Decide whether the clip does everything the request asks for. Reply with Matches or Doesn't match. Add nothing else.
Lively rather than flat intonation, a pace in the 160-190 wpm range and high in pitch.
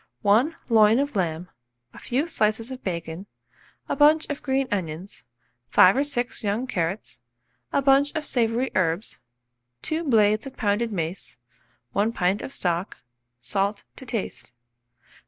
Doesn't match